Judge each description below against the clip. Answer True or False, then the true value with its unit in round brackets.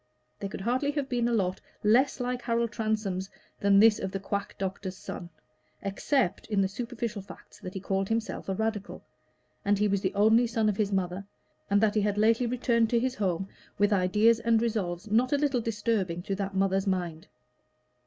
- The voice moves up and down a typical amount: True (3.2 semitones)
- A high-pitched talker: True (210 Hz)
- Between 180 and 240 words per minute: True (195 wpm)